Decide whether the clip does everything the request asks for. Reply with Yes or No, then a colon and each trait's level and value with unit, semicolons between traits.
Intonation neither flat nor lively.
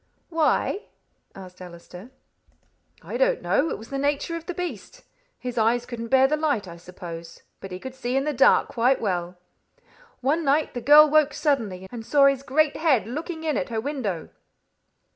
No: wide, 6.5 semitones